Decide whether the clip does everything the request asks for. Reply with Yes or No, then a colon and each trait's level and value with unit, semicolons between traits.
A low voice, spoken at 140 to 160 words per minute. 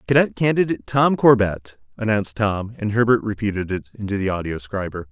Yes: low, 105 Hz; average, 155 wpm